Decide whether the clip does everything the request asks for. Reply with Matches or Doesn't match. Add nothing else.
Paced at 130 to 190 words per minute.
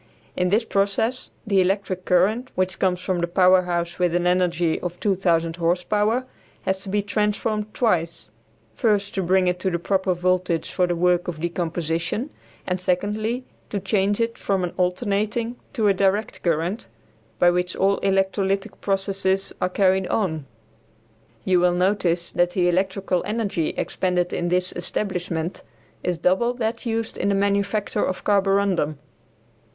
Matches